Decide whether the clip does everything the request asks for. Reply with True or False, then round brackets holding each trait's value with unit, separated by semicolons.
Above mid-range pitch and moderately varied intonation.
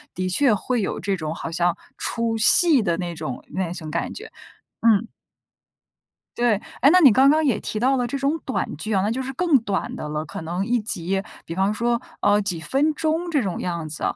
False (215 Hz; 6.9 semitones)